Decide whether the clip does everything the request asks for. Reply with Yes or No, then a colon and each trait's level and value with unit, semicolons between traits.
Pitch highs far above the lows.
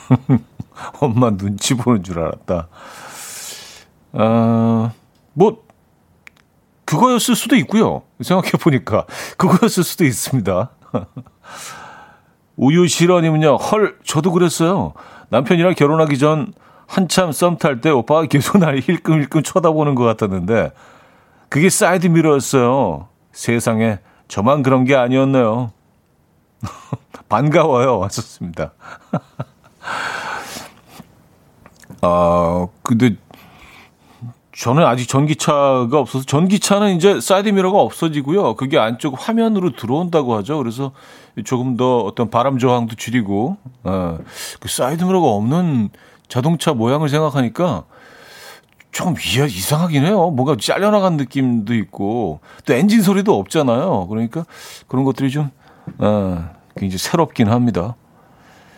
Yes: wide, 6.6 semitones